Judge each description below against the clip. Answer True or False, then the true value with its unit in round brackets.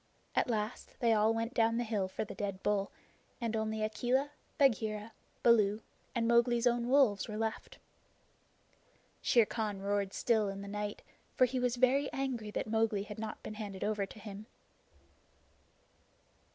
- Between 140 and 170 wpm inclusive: True (160 wpm)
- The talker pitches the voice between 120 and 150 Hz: False (220 Hz)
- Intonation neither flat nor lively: False (2.3 semitones)